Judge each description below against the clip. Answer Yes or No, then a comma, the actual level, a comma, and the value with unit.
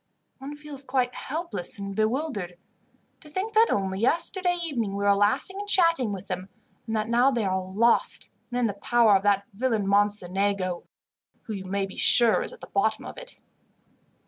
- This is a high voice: Yes, high, 220 Hz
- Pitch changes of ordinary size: No, wide, 5.7 semitones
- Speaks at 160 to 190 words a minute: Yes, average, 185 wpm